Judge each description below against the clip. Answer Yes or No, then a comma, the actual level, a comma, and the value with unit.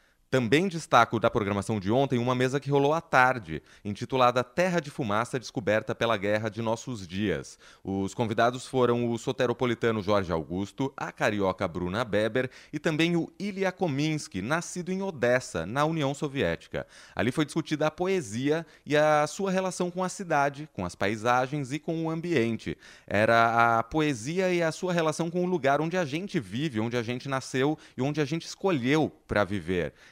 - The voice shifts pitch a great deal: Yes, wide, 5.7 semitones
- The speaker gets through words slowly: No, average, 175 wpm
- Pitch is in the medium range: No, low, 130 Hz